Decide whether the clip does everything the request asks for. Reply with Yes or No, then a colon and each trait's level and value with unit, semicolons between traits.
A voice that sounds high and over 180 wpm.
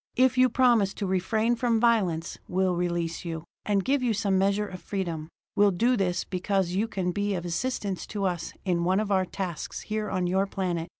Yes: high, 195 Hz; average, 200 wpm